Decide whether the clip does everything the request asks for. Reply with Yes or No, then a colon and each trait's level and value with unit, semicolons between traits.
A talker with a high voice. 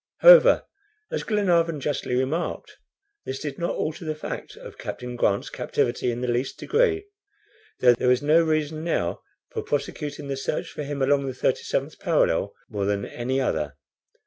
No: medium, 140 Hz